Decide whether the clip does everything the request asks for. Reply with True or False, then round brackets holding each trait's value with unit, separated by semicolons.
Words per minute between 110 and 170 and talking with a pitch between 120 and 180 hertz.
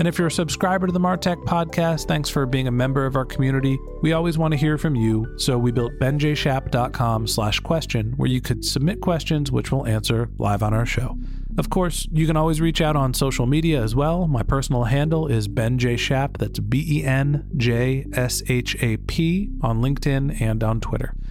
False (200 wpm; 135 Hz)